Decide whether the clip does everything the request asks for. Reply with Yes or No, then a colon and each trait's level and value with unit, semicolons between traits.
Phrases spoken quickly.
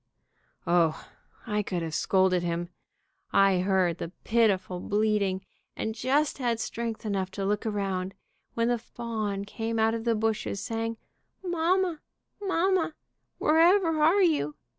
No: slow, 135 wpm